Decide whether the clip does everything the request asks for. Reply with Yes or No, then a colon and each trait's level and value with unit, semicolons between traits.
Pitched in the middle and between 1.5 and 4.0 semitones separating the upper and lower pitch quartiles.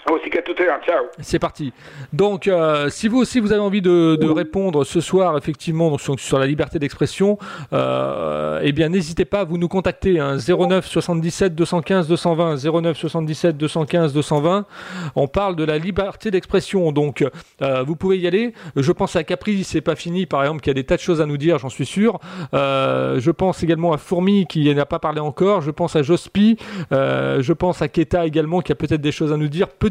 Yes: medium, 170 Hz; average, 3.7 semitones